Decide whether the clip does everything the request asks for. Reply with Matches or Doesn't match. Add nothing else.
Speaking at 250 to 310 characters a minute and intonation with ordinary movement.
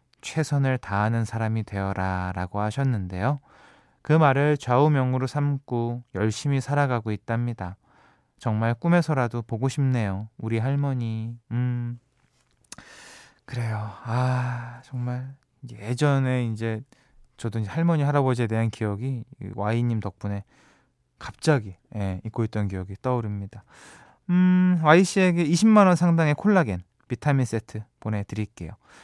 Matches